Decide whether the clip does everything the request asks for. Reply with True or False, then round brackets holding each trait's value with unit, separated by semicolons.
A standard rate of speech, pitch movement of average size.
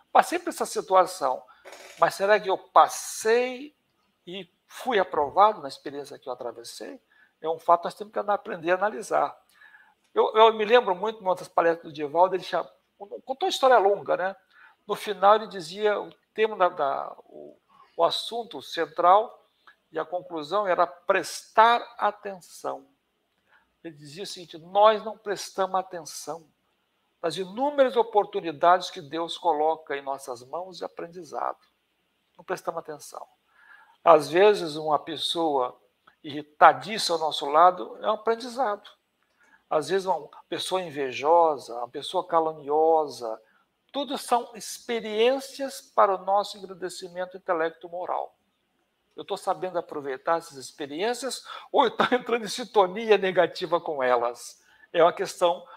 True (140 wpm; 4.7 semitones)